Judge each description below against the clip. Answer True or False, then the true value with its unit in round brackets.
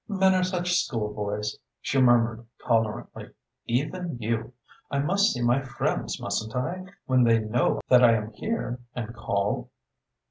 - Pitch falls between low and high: False (120 Hz)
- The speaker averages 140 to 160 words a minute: True (145 wpm)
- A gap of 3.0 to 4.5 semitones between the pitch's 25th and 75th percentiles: False (5.1 semitones)